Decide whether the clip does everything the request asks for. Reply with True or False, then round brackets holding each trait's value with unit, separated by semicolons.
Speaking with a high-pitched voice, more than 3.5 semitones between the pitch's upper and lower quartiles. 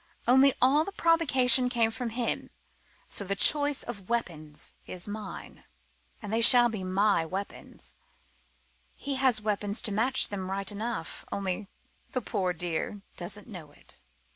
True (215 Hz; 4.4 semitones)